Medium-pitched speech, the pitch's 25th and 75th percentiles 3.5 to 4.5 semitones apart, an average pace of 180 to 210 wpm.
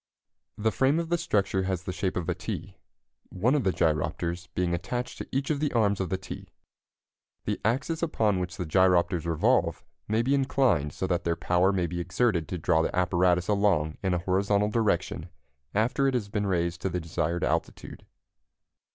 No: very low, 95 Hz; average, 4.1 semitones; average, 190 wpm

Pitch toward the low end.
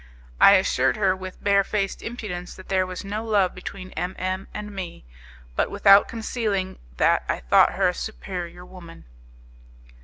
No: high, 190 Hz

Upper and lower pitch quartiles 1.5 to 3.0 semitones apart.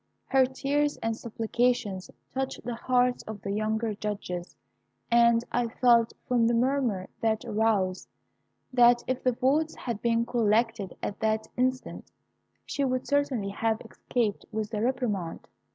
Yes: average, 2.7 semitones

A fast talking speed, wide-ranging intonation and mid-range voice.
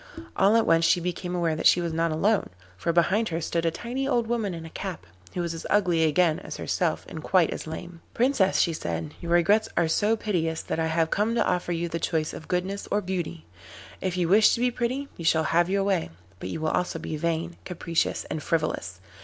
No: fast, 230 wpm; average, 3.4 semitones; medium, 170 Hz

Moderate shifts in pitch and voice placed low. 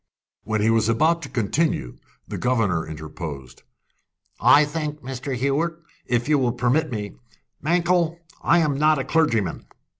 No: wide, 6.0 semitones; low, 130 Hz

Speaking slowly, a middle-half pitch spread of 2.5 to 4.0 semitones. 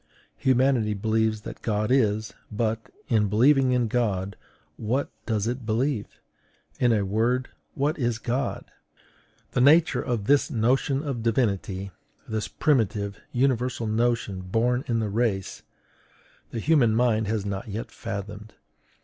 Yes: slow, 130 wpm; average, 3.0 semitones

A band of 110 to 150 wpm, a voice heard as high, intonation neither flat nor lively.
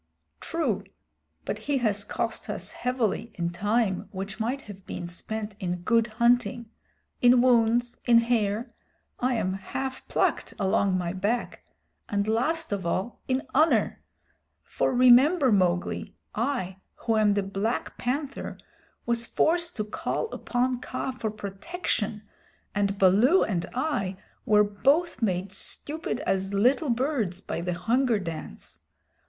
Yes: slow, 135 wpm; high, 225 Hz; average, 4.4 semitones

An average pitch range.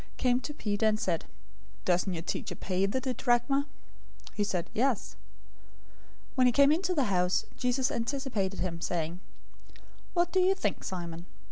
No: wide, 6.7 semitones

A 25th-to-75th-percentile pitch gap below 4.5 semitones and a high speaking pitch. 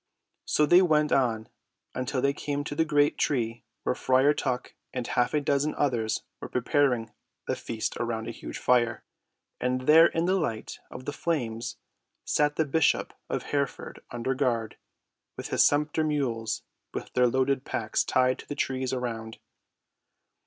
No: average, 3.7 semitones; low, 130 Hz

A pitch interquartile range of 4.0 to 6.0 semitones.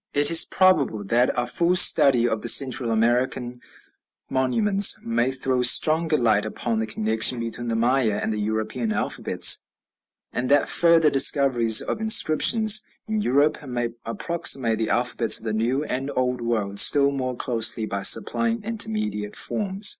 Yes: average, 5.2 semitones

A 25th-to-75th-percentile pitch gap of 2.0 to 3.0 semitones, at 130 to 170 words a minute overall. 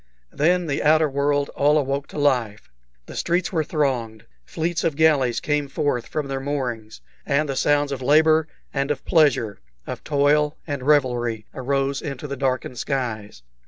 Yes: average, 2.7 semitones; average, 160 wpm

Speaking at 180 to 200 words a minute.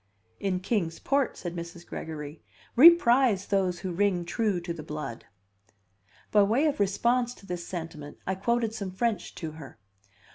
No: average, 160 wpm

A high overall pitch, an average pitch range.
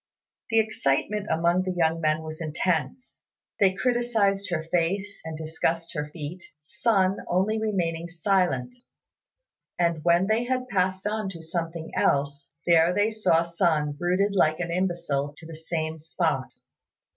No: medium, 170 Hz; average, 3.5 semitones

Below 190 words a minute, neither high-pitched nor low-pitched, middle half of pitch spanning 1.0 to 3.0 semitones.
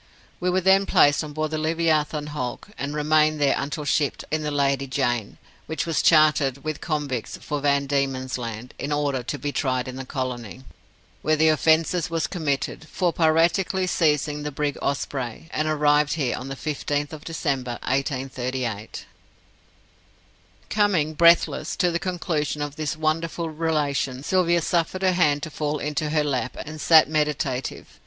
Yes: average, 160 wpm; medium, 150 Hz; narrow, 2.5 semitones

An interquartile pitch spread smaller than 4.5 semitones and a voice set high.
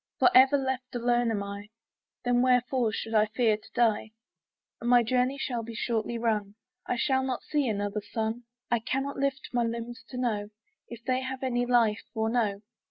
Yes: narrow, 2.5 semitones; high, 240 Hz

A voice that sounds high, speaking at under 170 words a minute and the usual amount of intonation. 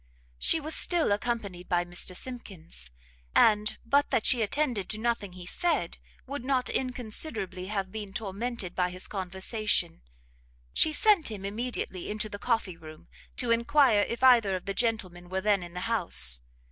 Yes: high, 210 Hz; average, 160 wpm; average, 4.7 semitones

